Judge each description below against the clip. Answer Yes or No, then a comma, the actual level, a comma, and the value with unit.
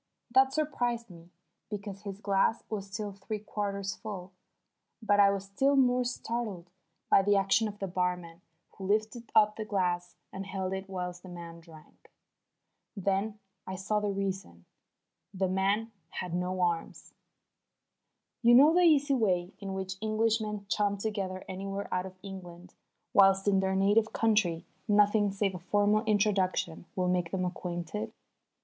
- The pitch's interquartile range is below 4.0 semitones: Yes, narrow, 2.5 semitones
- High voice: Yes, high, 195 Hz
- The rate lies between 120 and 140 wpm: No, average, 155 wpm